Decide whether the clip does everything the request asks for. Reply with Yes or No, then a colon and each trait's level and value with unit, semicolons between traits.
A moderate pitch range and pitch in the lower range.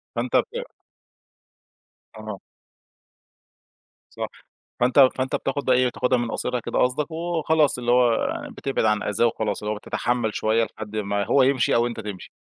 Yes: average, 3.1 semitones; low, 120 Hz